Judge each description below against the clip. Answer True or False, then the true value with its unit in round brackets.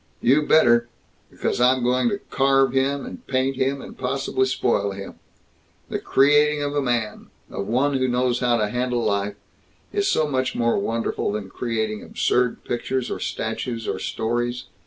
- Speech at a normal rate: True (165 wpm)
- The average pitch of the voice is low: True (125 Hz)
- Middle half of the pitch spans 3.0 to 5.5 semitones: False (2.6 semitones)